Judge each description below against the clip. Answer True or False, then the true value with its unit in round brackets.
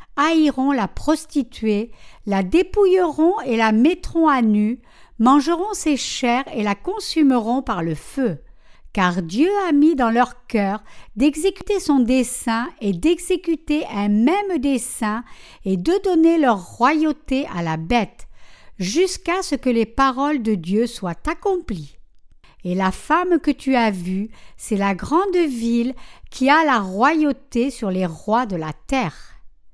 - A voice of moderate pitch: False (255 Hz)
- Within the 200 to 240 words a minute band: False (145 wpm)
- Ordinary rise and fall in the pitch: False (6.8 semitones)